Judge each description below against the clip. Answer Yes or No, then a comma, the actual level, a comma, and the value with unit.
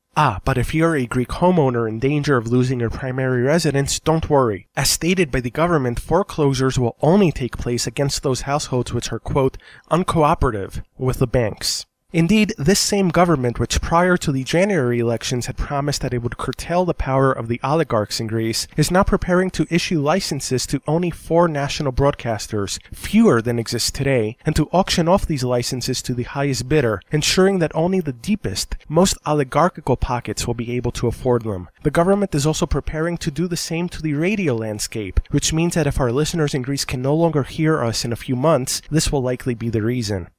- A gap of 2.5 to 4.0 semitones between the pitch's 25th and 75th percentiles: No, average, 5.1 semitones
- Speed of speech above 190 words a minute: Yes, average, 200 wpm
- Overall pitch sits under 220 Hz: Yes, medium, 140 Hz